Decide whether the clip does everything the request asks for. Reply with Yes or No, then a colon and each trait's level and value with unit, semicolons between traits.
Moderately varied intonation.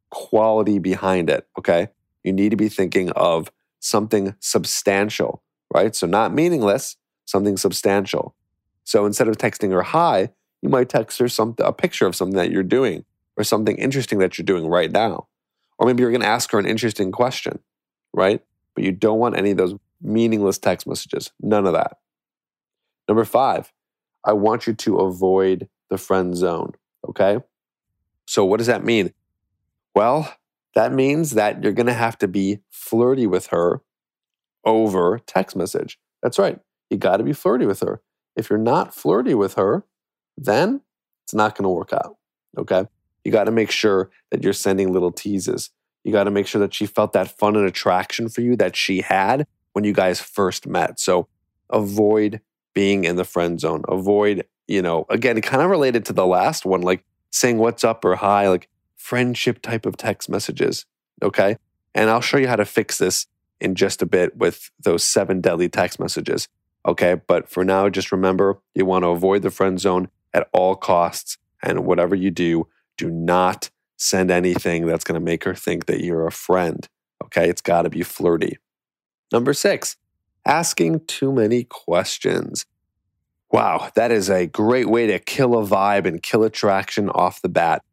Yes: average, 3.0 semitones